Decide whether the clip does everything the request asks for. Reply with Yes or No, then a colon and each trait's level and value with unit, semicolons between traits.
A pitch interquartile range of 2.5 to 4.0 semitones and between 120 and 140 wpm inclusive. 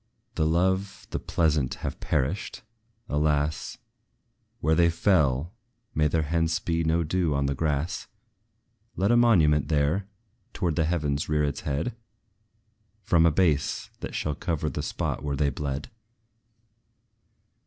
Yes: average, 2.8 semitones; slow, 135 wpm